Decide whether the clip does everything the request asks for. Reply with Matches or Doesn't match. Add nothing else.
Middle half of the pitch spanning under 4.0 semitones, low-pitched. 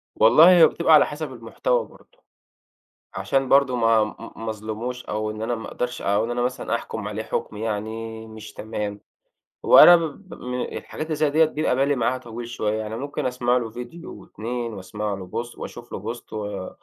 Matches